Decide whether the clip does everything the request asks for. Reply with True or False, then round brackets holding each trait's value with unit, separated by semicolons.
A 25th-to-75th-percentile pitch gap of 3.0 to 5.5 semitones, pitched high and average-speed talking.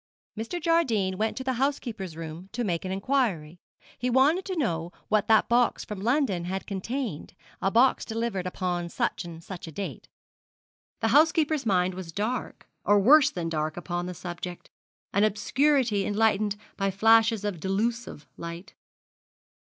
True (5.2 semitones; 205 Hz; 155 wpm)